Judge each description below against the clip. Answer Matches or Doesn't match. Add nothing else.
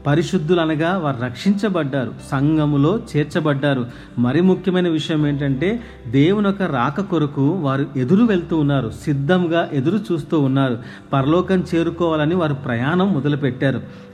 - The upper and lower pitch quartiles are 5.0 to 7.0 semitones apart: Doesn't match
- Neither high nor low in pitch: Matches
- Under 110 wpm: Doesn't match